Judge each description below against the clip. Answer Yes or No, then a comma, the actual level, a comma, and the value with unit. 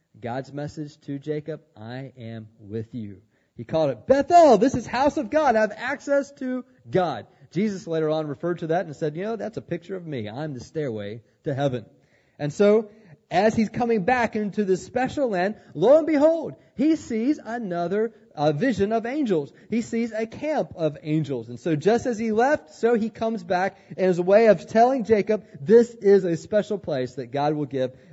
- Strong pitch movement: Yes, wide, 7.6 semitones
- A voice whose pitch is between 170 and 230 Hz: Yes, medium, 185 Hz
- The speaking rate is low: No, average, 200 wpm